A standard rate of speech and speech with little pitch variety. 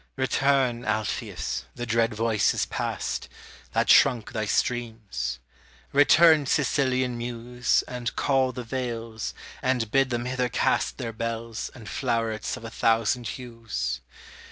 No: slow, 130 wpm; narrow, 2.2 semitones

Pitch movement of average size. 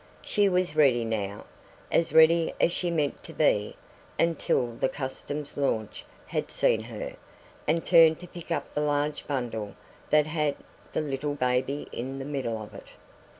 Yes: average, 4.1 semitones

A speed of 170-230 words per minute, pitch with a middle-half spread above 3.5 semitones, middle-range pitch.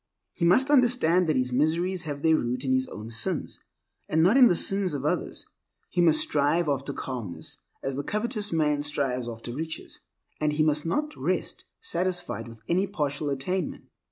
Yes: average, 180 wpm; average, 4.9 semitones; medium, 155 Hz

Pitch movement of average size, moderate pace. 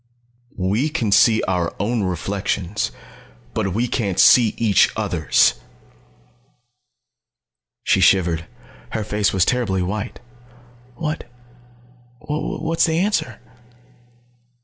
No: average, 4.7 semitones; slow, 105 wpm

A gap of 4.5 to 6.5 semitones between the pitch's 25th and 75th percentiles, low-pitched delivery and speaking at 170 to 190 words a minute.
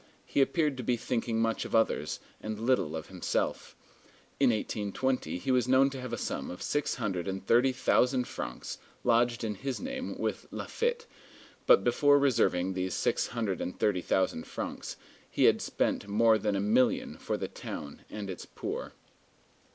Yes: average, 5.2 semitones; low, 115 Hz; average, 175 wpm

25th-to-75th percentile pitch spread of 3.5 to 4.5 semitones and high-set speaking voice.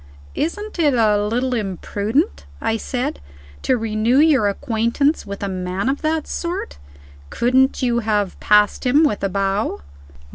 No: average, 5.3 semitones; high, 230 Hz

